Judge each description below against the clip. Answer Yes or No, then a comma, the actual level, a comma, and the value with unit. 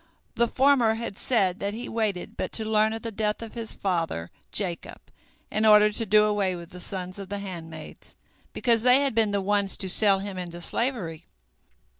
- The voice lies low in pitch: No, high, 205 Hz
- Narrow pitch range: No, average, 3.3 semitones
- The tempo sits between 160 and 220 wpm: Yes, average, 195 wpm